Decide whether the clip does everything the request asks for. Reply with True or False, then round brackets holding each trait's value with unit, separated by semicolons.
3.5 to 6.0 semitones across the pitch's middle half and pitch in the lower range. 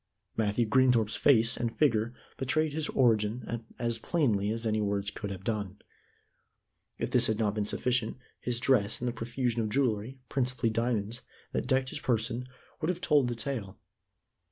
False (2.9 semitones; 115 Hz)